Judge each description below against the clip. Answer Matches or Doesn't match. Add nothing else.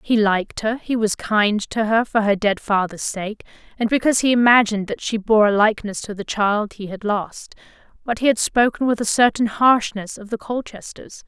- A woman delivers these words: Matches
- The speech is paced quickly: Matches